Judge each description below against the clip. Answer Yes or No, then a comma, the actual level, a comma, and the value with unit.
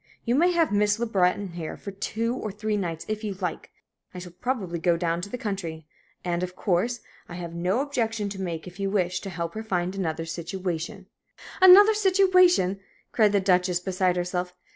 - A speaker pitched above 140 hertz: Yes, high, 190 Hz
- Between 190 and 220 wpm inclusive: Yes, average, 200 wpm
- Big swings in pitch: No, average, 3.8 semitones